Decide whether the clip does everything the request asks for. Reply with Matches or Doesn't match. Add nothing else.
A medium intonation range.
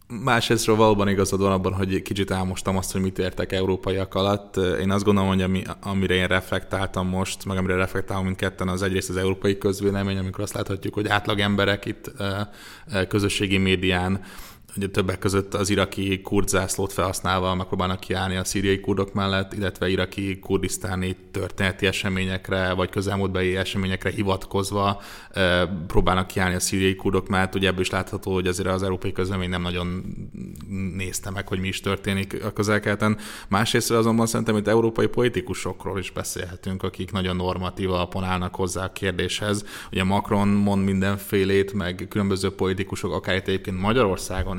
Doesn't match